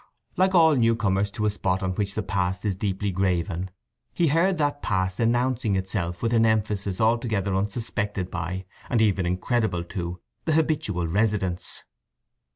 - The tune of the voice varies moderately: Yes, average, 3.7 semitones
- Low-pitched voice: Yes, low, 100 Hz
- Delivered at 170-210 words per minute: No, average, 155 wpm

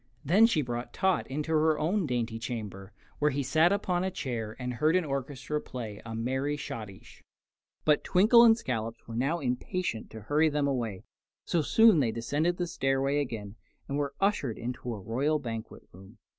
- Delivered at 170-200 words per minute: Yes, average, 180 wpm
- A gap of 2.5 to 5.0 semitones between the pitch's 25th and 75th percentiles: No, wide, 5.4 semitones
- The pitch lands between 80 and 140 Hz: Yes, low, 135 Hz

